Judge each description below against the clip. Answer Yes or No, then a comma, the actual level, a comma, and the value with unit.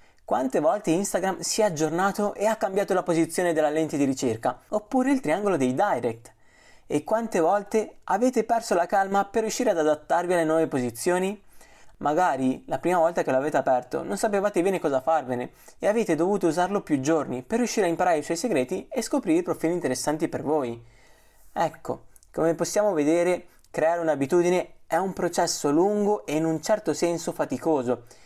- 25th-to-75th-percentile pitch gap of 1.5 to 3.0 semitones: No, average, 4.8 semitones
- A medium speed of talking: No, fast, 175 wpm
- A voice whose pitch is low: No, medium, 170 Hz